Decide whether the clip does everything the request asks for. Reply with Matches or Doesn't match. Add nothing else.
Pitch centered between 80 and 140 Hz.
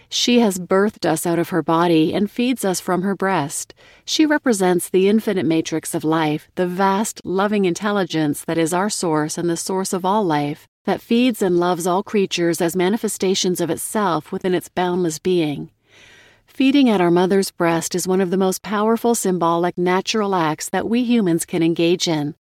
Doesn't match